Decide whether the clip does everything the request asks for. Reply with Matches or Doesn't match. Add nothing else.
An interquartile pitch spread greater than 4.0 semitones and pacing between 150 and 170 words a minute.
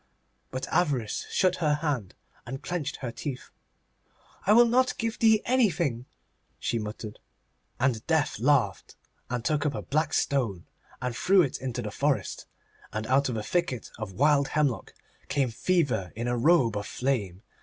Matches